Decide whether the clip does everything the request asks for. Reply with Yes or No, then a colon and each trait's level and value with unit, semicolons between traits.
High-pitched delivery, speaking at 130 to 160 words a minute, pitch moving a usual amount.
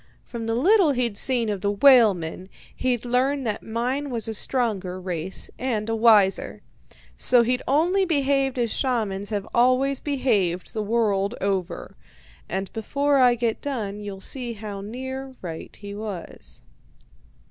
Yes: high, 230 Hz; average, 145 wpm; average, 4.4 semitones